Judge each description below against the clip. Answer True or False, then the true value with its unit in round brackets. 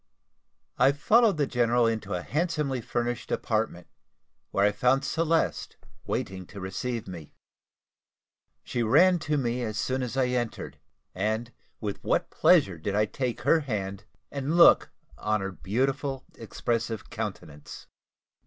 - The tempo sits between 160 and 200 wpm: False (135 wpm)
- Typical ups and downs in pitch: True (4.8 semitones)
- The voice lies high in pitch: False (120 Hz)